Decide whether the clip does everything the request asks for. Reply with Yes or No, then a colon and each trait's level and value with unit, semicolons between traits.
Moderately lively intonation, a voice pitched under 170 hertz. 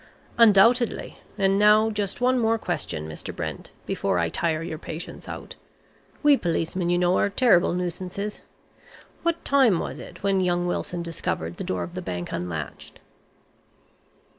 No: average, 4.7 semitones; medium, 180 Hz